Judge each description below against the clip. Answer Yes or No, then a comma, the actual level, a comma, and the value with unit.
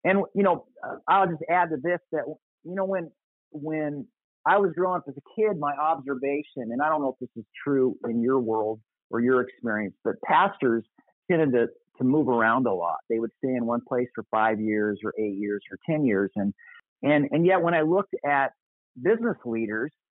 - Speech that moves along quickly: Yes, fast, 210 wpm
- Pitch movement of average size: No, wide, 6.5 semitones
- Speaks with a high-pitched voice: No, medium, 140 Hz